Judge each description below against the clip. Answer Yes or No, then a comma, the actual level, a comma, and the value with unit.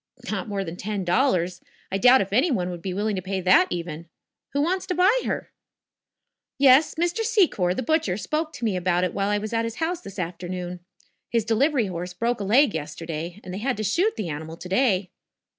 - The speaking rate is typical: No, fast, 215 wpm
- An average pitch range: No, wide, 6.5 semitones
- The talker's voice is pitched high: Yes, high, 200 Hz